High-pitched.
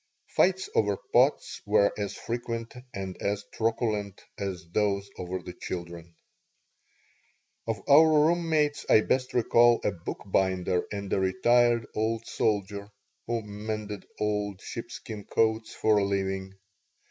No: low, 105 Hz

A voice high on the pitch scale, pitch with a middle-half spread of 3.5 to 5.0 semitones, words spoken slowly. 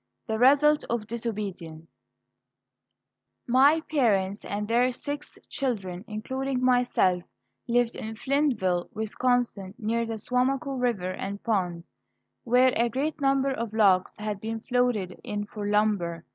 Yes: high, 230 Hz; average, 4.0 semitones; slow, 125 wpm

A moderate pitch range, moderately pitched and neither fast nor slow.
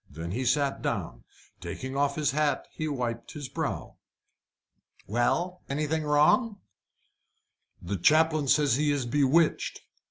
No: average, 3.1 semitones; medium, 145 Hz; slow, 125 wpm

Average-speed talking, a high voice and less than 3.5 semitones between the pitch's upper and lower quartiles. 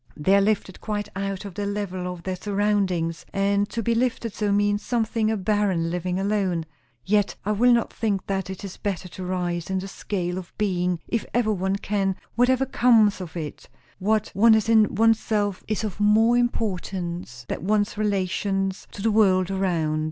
Yes: average, 185 wpm; high, 200 Hz; narrow, 2.6 semitones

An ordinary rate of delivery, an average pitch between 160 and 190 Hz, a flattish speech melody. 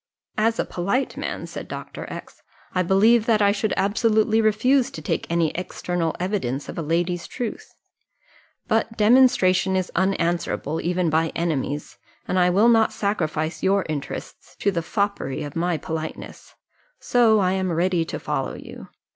No: average, 155 wpm; medium, 185 Hz; average, 4.5 semitones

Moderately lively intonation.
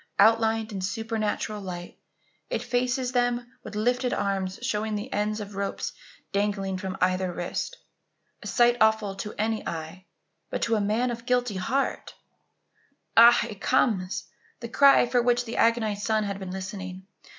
Yes: average, 3.5 semitones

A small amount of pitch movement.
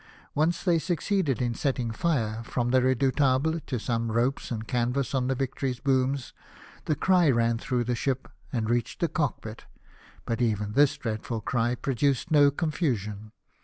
No: average, 3.5 semitones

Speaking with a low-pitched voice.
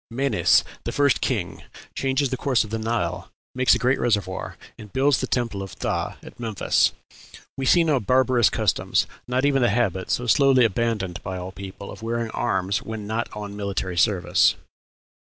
Yes: low, 115 Hz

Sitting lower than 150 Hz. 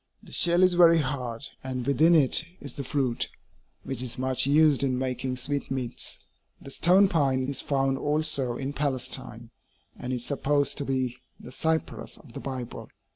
Yes: low, 135 Hz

